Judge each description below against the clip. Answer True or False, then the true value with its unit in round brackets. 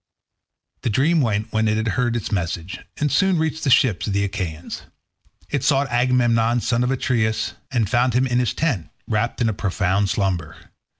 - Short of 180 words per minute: False (185 wpm)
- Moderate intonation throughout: True (3.8 semitones)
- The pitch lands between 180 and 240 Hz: False (115 Hz)